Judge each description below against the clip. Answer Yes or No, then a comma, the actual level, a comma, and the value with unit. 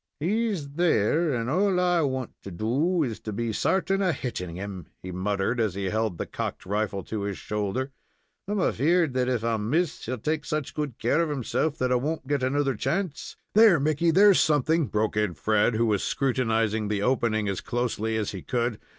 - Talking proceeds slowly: No, average, 200 wpm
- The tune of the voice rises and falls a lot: Yes, wide, 6.5 semitones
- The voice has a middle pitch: No, low, 125 Hz